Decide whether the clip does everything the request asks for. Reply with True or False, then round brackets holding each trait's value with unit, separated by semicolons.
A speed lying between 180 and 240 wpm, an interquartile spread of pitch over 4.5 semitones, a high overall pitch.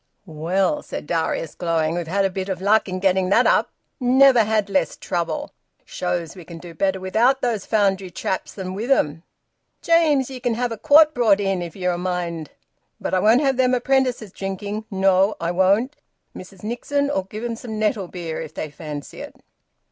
True (190 wpm; 5.1 semitones; 195 Hz)